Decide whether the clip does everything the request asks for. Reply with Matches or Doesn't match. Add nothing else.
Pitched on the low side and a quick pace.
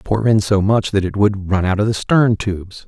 Matches